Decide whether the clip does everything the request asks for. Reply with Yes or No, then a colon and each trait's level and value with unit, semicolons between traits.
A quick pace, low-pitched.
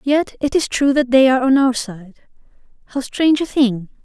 No: fast, 210 wpm; very high, 260 Hz